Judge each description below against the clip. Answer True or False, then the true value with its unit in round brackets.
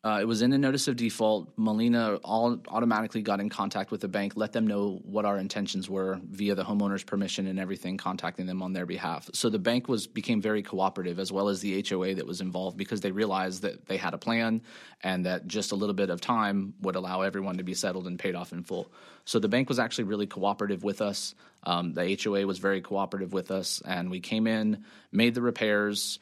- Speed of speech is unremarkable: False (230 wpm)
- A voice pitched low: True (100 Hz)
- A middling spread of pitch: False (2.2 semitones)